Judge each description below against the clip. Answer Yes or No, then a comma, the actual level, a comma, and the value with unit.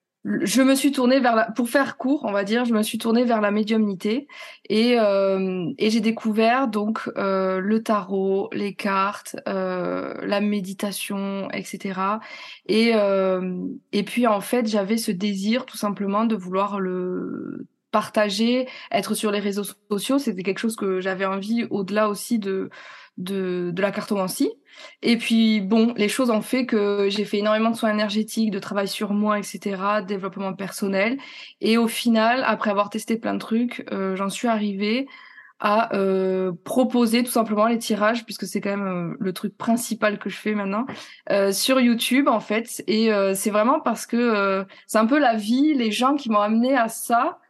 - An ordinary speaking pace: Yes, average, 185 wpm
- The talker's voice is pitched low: No, high, 215 Hz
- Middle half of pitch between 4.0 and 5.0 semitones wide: No, average, 2.7 semitones